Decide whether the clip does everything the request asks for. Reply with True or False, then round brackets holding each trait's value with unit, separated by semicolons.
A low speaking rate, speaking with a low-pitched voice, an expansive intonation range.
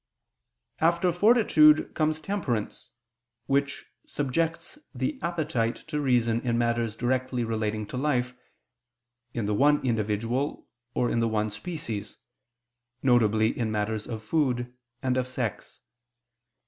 False (120 wpm; 125 Hz; 4.9 semitones)